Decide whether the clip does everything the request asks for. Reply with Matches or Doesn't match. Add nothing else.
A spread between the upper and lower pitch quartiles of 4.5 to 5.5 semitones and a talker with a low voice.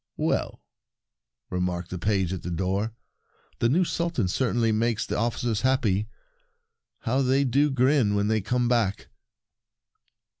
Matches